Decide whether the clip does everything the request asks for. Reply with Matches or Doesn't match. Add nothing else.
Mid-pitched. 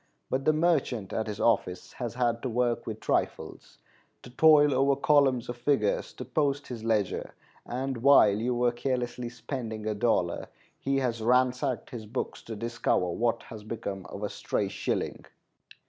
Doesn't match